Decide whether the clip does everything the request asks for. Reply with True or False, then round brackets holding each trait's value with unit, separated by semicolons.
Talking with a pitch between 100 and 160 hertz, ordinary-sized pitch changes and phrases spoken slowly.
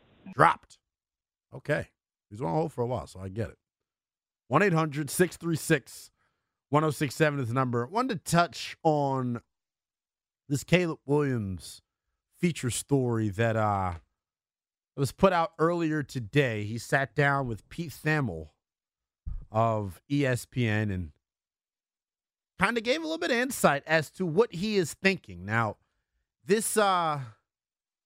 False (140 Hz; 6.9 semitones; 130 wpm)